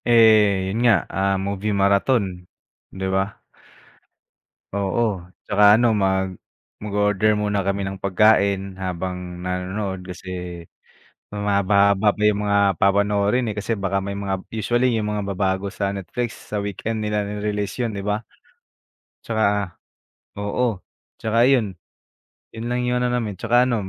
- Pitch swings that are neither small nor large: No, narrow, 1.9 semitones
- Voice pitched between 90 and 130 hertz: Yes, low, 100 Hz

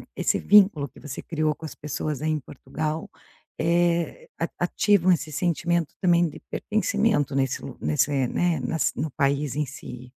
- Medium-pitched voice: Yes, medium, 155 Hz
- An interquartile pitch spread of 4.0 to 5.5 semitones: No, average, 3.5 semitones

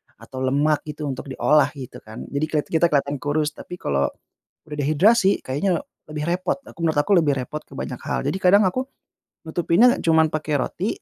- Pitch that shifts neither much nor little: Yes, average, 3.5 semitones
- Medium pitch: Yes, medium, 150 Hz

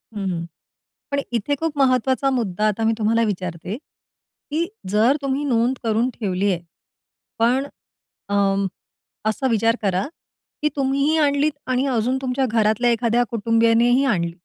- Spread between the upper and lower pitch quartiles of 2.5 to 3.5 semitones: No, average, 4.1 semitones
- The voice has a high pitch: Yes, high, 230 Hz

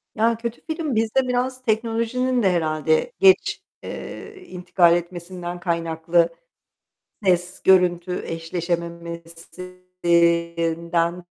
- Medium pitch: Yes, medium, 175 Hz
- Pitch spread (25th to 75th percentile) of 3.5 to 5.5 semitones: Yes, average, 4.8 semitones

